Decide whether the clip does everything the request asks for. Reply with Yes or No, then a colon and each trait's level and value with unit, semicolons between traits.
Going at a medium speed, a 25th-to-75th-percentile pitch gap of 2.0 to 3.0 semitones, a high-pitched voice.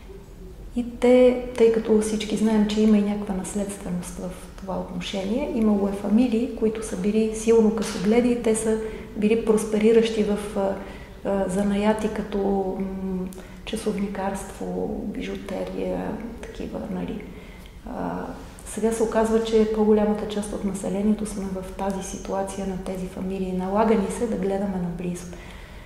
Yes: average, 135 wpm; narrow, 2.5 semitones; high, 210 Hz